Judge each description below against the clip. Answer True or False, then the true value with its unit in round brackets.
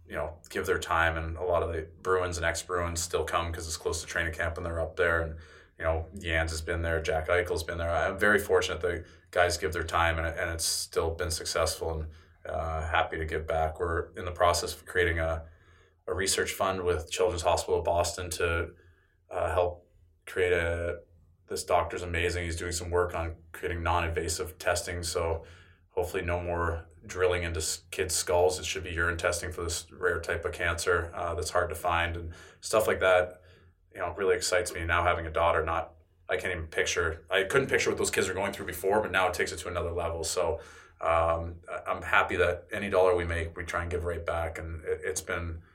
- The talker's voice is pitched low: True (85 Hz)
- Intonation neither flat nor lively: False (1.3 semitones)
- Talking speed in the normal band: False (220 wpm)